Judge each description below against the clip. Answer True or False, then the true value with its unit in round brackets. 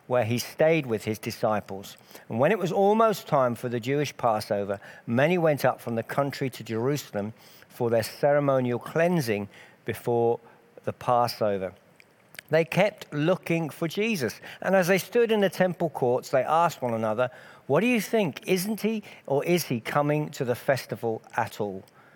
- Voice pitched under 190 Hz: True (140 Hz)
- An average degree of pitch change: False (6.9 semitones)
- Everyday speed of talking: True (170 wpm)